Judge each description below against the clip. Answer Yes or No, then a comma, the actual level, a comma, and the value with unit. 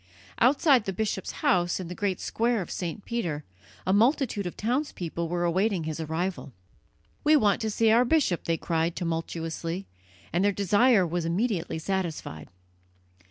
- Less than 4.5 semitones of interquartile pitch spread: No, average, 4.8 semitones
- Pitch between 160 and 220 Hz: Yes, medium, 185 Hz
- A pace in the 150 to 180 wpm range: Yes, average, 155 wpm